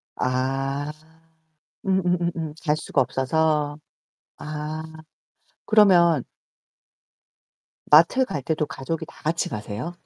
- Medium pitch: Yes, medium, 155 Hz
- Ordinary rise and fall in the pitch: Yes, average, 3.7 semitones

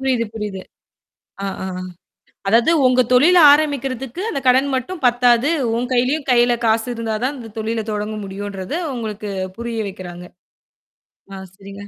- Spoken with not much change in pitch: No, average, 3.7 semitones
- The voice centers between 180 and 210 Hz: No, high, 235 Hz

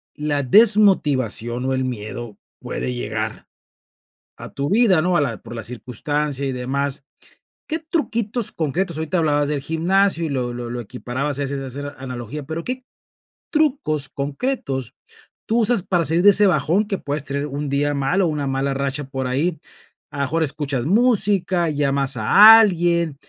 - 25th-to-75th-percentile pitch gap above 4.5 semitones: Yes, average, 5.2 semitones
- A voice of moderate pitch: Yes, medium, 145 Hz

